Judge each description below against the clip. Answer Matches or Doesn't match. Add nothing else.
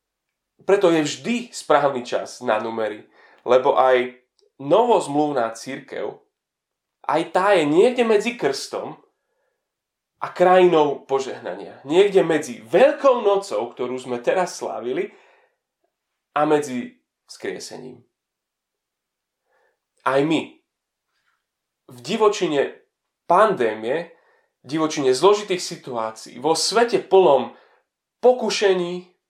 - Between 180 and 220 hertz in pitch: Matches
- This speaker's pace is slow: Matches